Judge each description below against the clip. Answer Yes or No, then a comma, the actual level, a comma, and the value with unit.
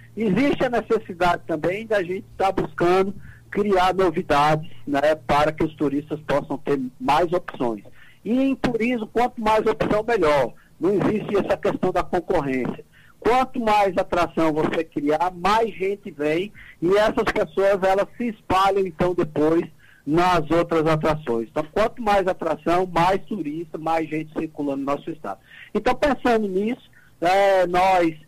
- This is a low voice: No, medium, 180 Hz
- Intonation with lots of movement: No, average, 4.6 semitones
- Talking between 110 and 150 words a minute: Yes, average, 145 wpm